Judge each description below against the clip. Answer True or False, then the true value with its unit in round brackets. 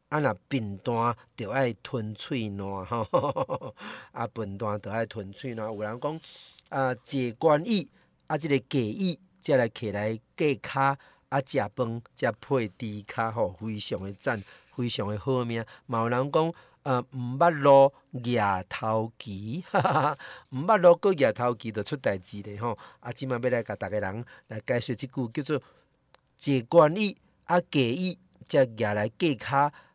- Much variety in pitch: False (4.3 semitones)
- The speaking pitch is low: True (125 Hz)